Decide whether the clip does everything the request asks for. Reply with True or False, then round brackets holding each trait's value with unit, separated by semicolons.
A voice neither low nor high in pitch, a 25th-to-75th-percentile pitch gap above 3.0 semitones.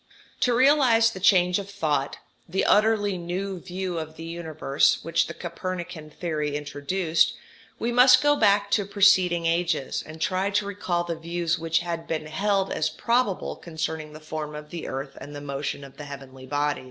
True (170 Hz; 4.4 semitones)